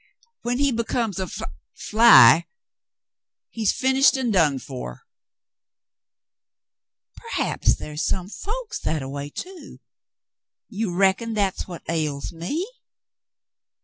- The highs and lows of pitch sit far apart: Yes, wide, 7.7 semitones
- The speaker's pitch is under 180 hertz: No, high, 195 Hz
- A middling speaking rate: No, slow, 115 wpm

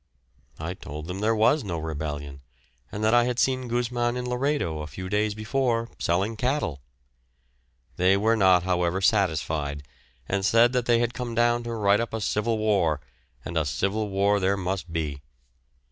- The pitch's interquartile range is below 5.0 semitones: No, wide, 5.5 semitones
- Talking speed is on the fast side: No, average, 175 wpm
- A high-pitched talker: No, low, 100 Hz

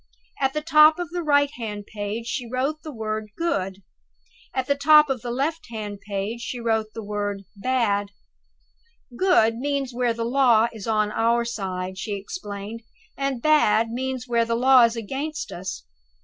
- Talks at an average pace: Yes, average, 170 wpm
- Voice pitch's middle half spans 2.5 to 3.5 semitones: No, average, 4.4 semitones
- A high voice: Yes, high, 235 Hz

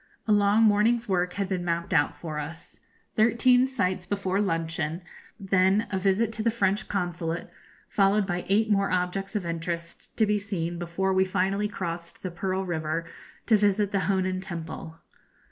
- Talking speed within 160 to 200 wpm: Yes, average, 165 wpm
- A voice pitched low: No, high, 190 Hz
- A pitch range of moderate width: Yes, average, 3.1 semitones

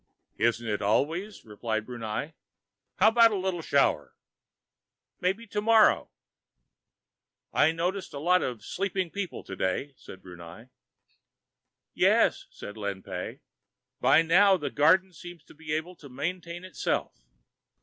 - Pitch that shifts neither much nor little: No, wide, 8.9 semitones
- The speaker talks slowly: Yes, slow, 125 wpm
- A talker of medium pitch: Yes, medium, 160 Hz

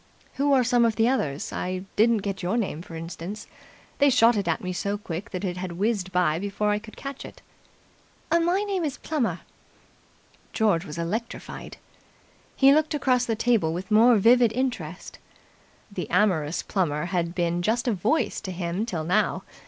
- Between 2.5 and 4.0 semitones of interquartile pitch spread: No, average, 5.2 semitones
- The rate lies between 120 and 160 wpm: No, average, 175 wpm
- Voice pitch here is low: No, high, 205 Hz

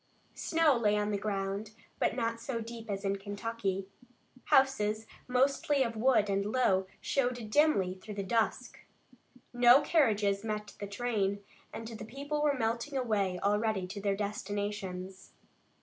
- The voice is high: Yes, high, 215 Hz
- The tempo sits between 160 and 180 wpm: No, average, 145 wpm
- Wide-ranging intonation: No, average, 3.3 semitones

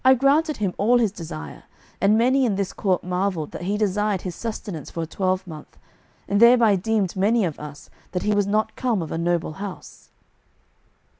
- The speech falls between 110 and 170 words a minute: No, average, 190 wpm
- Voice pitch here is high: Yes, high, 200 Hz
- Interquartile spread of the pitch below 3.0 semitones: No, average, 3.8 semitones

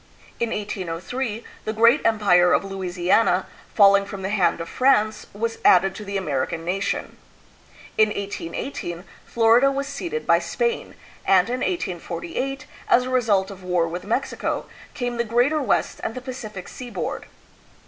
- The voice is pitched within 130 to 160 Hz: No, high, 210 Hz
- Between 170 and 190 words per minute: No, average, 150 wpm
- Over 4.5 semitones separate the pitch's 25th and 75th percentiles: Yes, average, 5.0 semitones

